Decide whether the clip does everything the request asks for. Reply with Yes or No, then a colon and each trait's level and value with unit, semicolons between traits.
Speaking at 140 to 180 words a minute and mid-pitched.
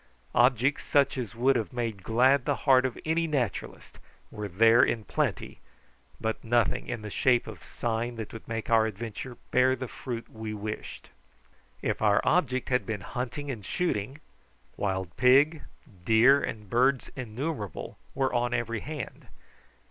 No: average, 155 wpm; low, 120 Hz